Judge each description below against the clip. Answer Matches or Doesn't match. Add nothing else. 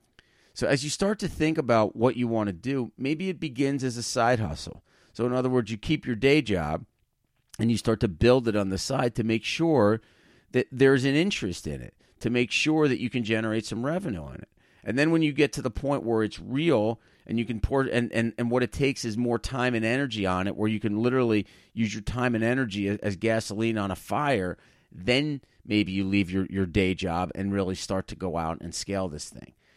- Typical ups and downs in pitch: Matches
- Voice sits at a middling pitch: Doesn't match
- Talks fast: Matches